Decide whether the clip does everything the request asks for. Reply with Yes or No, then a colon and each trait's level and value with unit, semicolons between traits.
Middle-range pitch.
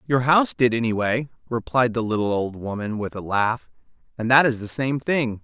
No: low, 120 Hz